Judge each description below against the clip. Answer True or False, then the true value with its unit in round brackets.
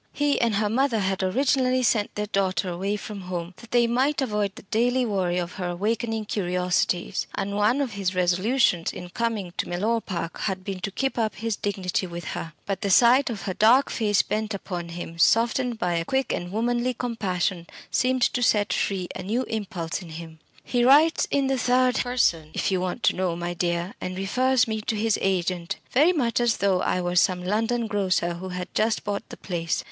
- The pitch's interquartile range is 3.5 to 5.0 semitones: True (4.6 semitones)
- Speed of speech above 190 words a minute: True (205 wpm)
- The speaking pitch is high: True (205 Hz)